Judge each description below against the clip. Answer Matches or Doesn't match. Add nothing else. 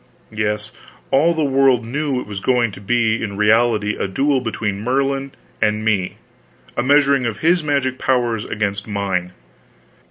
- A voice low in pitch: Matches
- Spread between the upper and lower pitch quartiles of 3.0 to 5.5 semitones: Matches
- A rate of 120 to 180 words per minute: Matches